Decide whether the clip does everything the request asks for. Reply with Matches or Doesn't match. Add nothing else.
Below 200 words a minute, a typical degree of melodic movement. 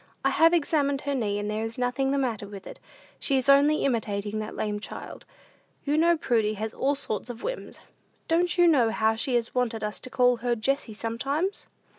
Doesn't match